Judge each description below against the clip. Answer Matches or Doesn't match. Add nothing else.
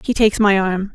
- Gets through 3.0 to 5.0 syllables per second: Doesn't match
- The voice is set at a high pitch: Matches